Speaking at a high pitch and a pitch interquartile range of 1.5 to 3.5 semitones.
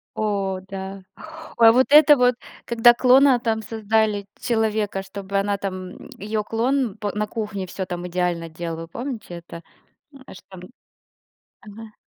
Yes: high, 210 Hz; average, 3.0 semitones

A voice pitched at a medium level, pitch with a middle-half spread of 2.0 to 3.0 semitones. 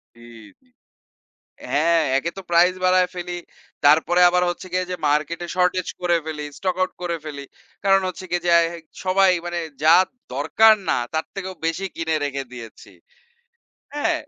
Yes: medium, 175 Hz; narrow, 2.5 semitones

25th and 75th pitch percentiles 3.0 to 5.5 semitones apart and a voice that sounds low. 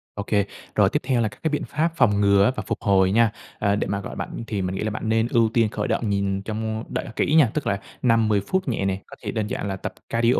No: narrow, 2.6 semitones; low, 110 Hz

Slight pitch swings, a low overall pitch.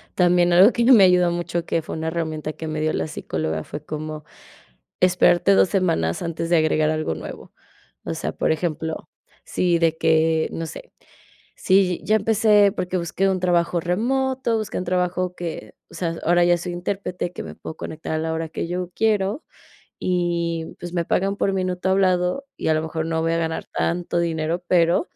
No: narrow, 2.3 semitones; medium, 175 Hz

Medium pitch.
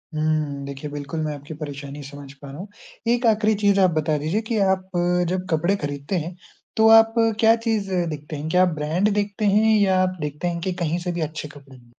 Yes: medium, 165 Hz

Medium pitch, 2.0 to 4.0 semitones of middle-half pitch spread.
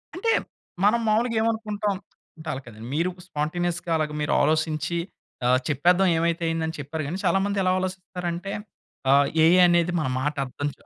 Yes: medium, 170 Hz; average, 3.7 semitones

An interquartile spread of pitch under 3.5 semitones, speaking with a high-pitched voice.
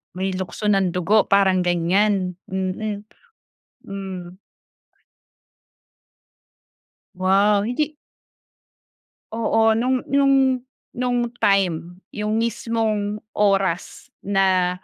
Yes: average, 3.1 semitones; high, 200 Hz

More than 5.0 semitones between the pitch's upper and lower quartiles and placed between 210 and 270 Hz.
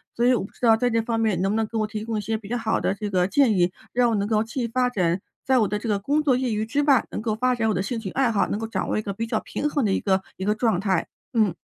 No: average, 3.0 semitones; high, 220 Hz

